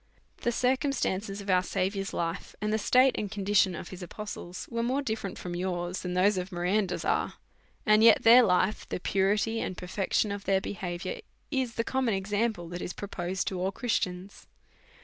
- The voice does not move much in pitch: No, average, 3.3 semitones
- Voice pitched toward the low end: No, high, 195 Hz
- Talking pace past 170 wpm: Yes, average, 190 wpm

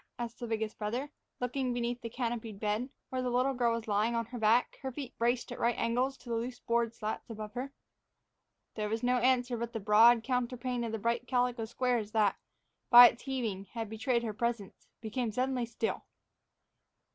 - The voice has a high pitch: Yes, high, 235 Hz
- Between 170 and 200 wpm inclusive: Yes, average, 190 wpm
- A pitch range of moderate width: No, narrow, 1.9 semitones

